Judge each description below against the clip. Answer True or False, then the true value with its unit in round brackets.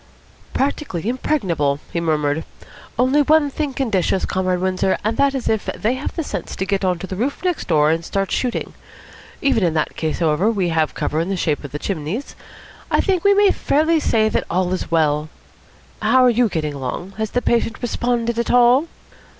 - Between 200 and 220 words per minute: True (205 wpm)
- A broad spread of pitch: True (7.5 semitones)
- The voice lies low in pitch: False (200 Hz)